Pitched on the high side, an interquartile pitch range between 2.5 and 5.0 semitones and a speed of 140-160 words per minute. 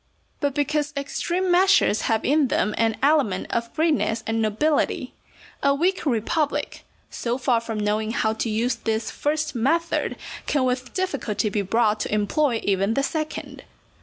No: very high, 250 Hz; wide, 5.5 semitones; average, 155 wpm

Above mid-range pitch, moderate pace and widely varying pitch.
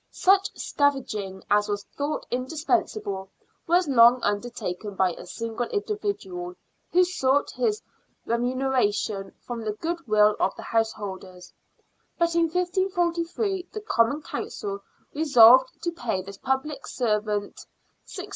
No: very high, 255 Hz; slow, 120 wpm; wide, 8.5 semitones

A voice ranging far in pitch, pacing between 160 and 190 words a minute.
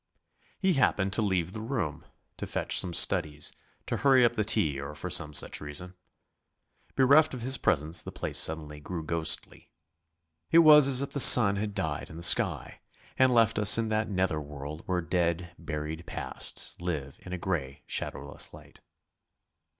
Yes: wide, 6.6 semitones; average, 175 wpm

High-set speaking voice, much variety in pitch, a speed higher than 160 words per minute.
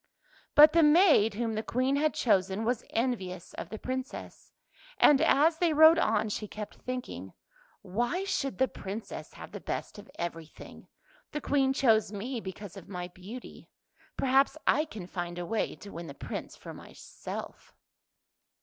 Yes: high, 230 Hz; wide, 6.2 semitones; average, 170 wpm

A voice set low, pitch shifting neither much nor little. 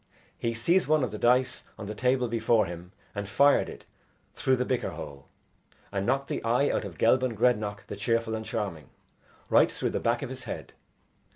Yes: low, 115 Hz; average, 3.7 semitones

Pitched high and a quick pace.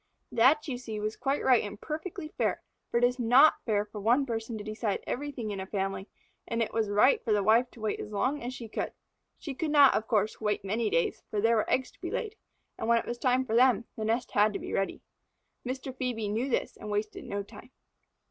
Yes: high, 230 Hz; fast, 240 wpm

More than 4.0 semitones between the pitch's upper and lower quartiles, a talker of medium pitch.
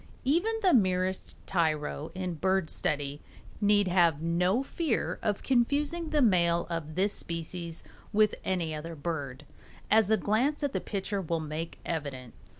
Yes: average, 5.0 semitones; medium, 180 Hz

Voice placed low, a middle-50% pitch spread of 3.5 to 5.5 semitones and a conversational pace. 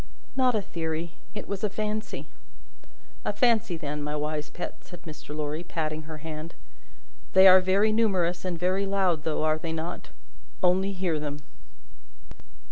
No: medium, 175 Hz; average, 3.8 semitones; average, 155 wpm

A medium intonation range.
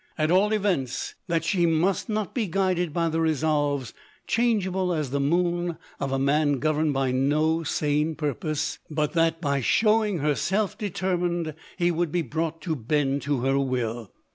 Yes: average, 3.6 semitones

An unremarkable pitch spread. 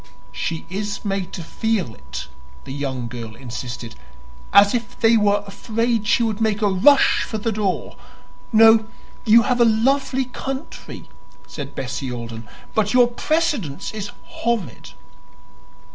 No: wide, 8.5 semitones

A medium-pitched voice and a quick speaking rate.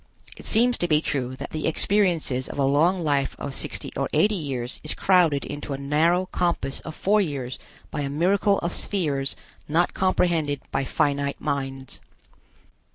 No: medium, 150 Hz; average, 165 wpm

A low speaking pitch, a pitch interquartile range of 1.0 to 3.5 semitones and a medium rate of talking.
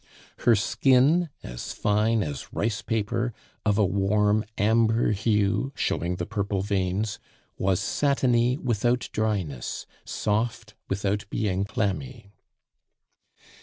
No: low, 105 Hz; average, 2.8 semitones; slow, 105 wpm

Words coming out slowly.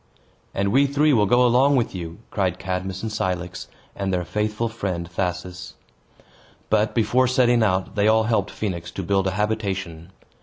No: average, 165 wpm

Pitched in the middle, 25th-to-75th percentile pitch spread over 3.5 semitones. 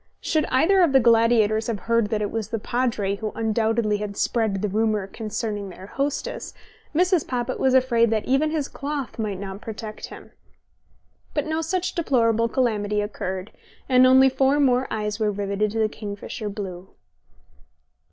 No: high, 225 Hz; average, 4.0 semitones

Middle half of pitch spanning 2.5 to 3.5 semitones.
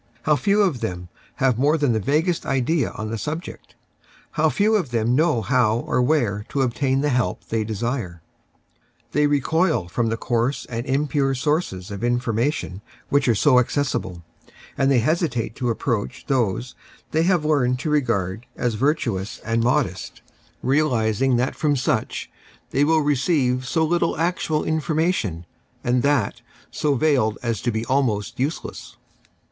No: average, 4.7 semitones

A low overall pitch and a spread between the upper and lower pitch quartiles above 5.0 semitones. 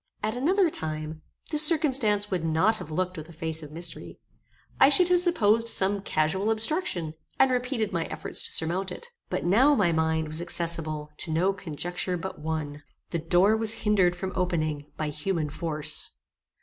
No: medium, 180 Hz; wide, 5.6 semitones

